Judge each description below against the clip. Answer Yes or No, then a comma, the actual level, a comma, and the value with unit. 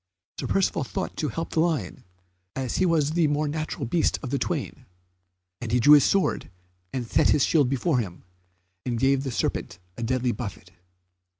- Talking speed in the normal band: Yes, average, 185 wpm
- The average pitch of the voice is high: No, low, 135 Hz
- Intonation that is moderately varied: Yes, average, 4.3 semitones